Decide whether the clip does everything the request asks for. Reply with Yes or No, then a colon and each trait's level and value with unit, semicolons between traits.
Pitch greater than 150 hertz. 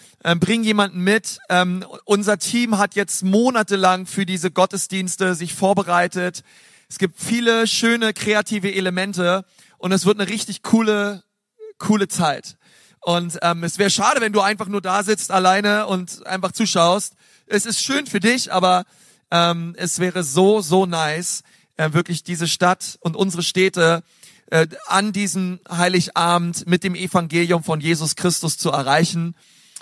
Yes: medium, 185 Hz